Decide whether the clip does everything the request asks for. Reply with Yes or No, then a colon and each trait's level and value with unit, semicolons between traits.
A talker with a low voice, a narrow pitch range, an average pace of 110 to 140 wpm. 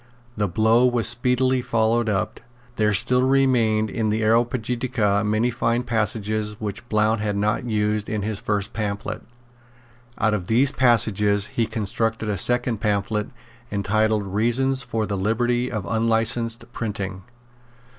Yes: low, 110 Hz; narrow, 2.2 semitones; slow, 135 wpm